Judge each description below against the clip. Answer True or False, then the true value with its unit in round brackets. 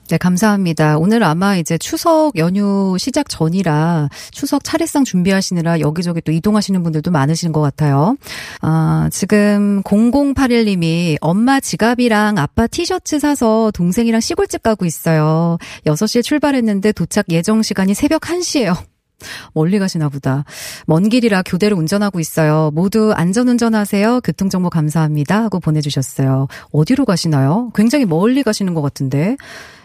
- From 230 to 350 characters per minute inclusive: True (335 characters per minute)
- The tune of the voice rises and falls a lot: True (6.1 semitones)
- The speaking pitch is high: True (195 Hz)